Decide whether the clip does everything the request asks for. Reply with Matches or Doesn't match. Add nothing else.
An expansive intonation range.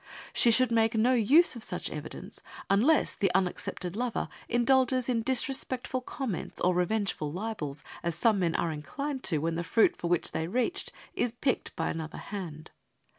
Matches